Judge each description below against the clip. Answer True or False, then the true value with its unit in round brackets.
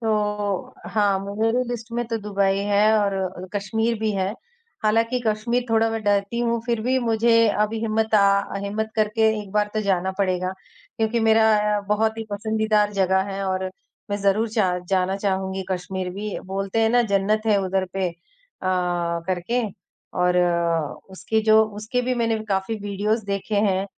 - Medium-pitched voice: False (210 Hz)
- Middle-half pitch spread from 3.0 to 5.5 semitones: False (2.4 semitones)